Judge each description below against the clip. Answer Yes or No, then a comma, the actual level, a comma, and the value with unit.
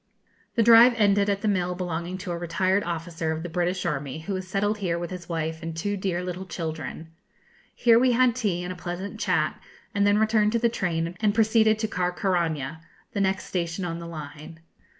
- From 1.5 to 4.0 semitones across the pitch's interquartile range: Yes, average, 3.5 semitones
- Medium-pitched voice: Yes, medium, 180 Hz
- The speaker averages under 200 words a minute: No, fast, 205 wpm